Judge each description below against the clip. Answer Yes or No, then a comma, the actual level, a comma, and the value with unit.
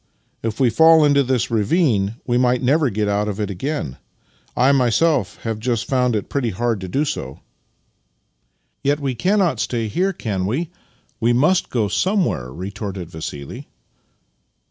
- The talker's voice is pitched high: No, low, 120 Hz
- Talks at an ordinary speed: Yes, average, 160 wpm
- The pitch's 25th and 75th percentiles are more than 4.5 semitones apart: Yes, wide, 5.5 semitones